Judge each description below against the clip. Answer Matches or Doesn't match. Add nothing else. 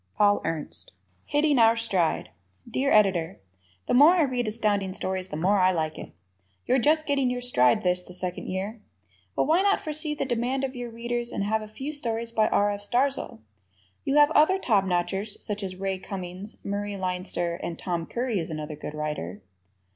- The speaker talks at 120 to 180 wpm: Doesn't match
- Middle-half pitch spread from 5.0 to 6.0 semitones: Matches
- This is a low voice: Doesn't match